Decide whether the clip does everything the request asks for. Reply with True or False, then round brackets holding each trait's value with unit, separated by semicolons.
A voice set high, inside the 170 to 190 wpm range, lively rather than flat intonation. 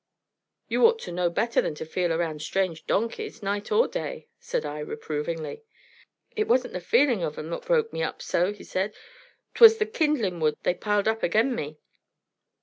True (200 Hz; 185 wpm; 8.8 semitones)